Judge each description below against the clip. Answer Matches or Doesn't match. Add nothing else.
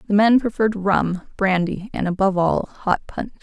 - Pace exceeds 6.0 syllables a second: Doesn't match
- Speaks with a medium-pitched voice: Doesn't match